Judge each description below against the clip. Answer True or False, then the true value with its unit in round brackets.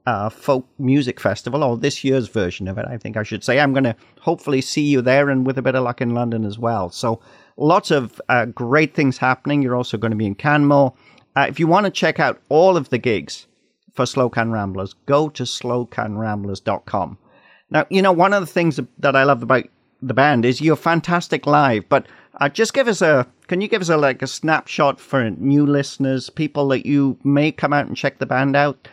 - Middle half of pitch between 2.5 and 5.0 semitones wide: True (3.3 semitones)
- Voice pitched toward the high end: False (135 Hz)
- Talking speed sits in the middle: False (225 wpm)